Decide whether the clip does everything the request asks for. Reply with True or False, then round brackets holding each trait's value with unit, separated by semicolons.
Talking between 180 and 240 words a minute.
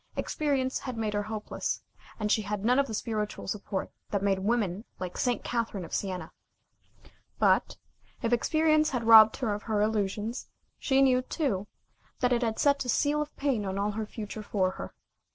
True (185 wpm)